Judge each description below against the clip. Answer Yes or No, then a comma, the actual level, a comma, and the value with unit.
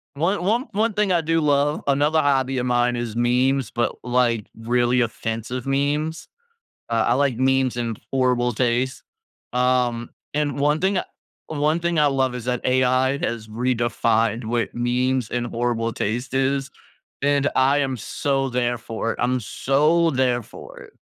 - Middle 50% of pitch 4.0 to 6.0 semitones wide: No, average, 2.9 semitones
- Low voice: Yes, low, 130 Hz